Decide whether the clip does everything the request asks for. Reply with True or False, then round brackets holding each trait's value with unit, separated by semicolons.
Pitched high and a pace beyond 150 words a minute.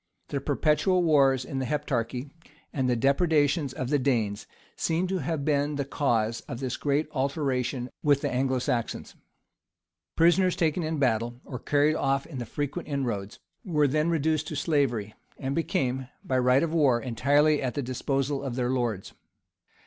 False (140 Hz; 165 wpm)